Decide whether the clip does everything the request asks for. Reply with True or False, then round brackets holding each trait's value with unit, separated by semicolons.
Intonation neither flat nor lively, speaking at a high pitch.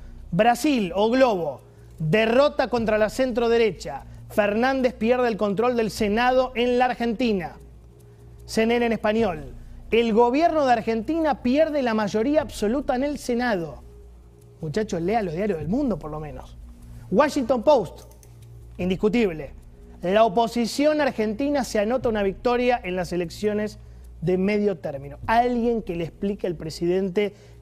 False (6.3 semitones; 215 Hz)